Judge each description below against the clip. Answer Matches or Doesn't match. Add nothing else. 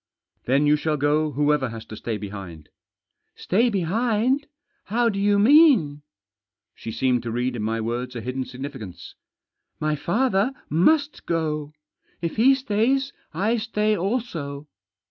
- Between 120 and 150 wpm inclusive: Doesn't match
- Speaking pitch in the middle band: Matches